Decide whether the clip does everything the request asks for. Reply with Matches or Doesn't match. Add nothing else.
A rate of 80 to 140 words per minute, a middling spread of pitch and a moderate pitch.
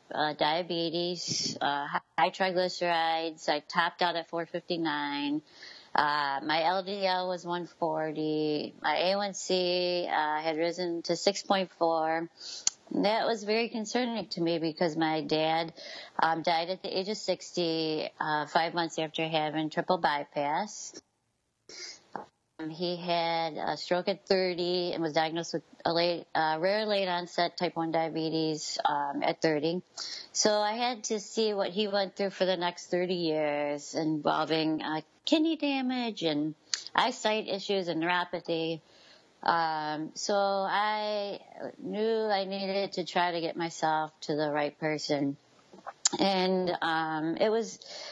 Matches